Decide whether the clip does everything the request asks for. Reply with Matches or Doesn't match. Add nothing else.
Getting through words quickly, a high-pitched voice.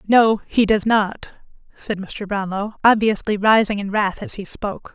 Doesn't match